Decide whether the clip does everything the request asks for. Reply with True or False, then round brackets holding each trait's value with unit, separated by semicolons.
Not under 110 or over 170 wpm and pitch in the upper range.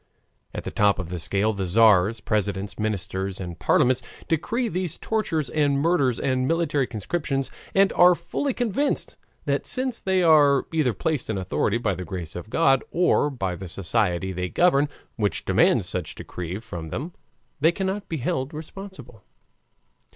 False (160 wpm; 130 Hz)